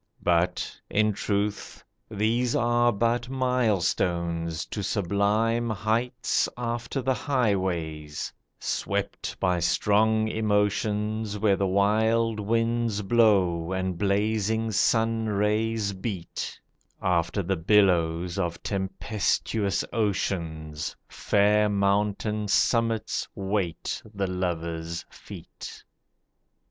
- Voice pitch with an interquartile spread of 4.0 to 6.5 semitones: No, average, 3.3 semitones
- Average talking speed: No, slow, 90 wpm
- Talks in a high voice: No, low, 105 Hz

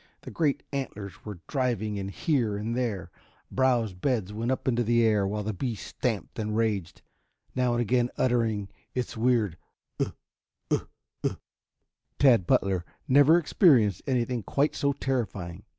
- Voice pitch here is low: Yes, low, 115 Hz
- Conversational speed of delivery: Yes, average, 150 wpm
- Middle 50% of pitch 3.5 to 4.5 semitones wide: Yes, average, 3.8 semitones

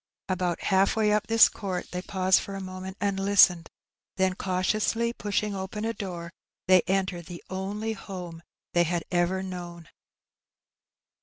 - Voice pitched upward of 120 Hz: Yes, high, 190 Hz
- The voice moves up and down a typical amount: No, narrow, 2.0 semitones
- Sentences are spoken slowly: No, average, 150 wpm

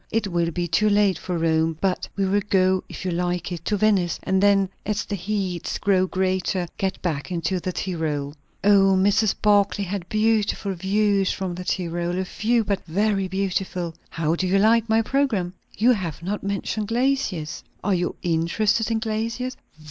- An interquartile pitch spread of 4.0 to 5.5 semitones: No, average, 2.9 semitones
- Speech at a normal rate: Yes, average, 180 wpm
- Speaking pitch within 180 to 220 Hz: Yes, high, 190 Hz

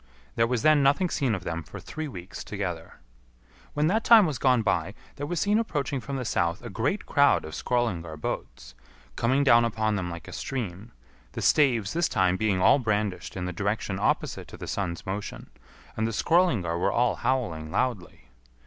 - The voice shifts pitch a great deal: Yes, wide, 6.9 semitones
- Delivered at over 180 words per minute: Yes, average, 190 wpm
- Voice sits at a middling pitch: No, low, 115 Hz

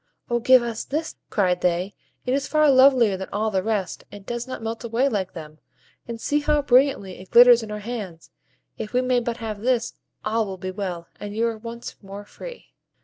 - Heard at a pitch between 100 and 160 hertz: No, high, 225 Hz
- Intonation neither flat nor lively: Yes, average, 3.9 semitones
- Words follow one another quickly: Yes, fast, 210 wpm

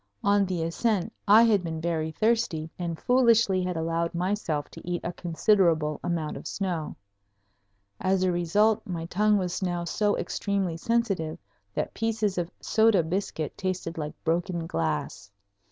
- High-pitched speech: No, medium, 180 Hz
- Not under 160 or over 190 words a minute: No, average, 150 wpm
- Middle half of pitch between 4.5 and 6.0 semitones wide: No, average, 3.8 semitones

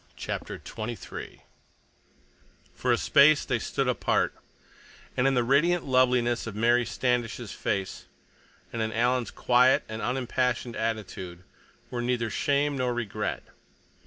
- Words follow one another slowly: Yes, slow, 125 wpm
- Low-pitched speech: Yes, low, 120 Hz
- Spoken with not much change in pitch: Yes, narrow, 2.0 semitones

